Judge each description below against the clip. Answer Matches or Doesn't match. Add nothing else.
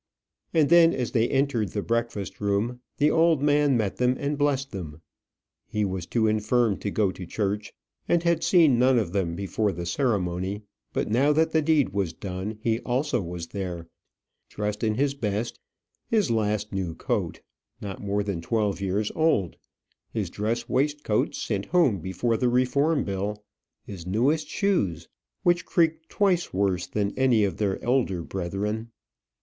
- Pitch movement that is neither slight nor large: Doesn't match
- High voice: Doesn't match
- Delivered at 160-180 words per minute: Matches